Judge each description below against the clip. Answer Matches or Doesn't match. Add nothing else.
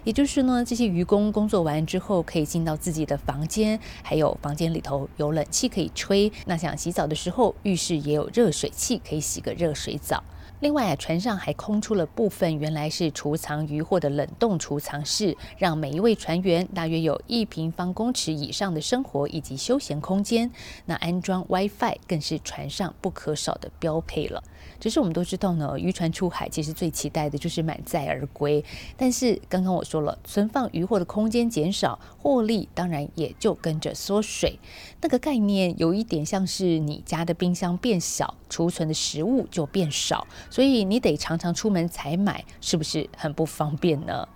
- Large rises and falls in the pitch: Doesn't match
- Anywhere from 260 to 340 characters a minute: Matches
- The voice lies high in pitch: Doesn't match